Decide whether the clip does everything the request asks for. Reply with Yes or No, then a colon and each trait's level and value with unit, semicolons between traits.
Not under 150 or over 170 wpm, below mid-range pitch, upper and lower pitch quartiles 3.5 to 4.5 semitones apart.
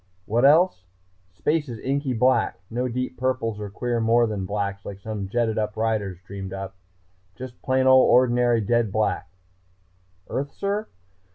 Yes: average, 155 wpm; low, 115 Hz; average, 4.0 semitones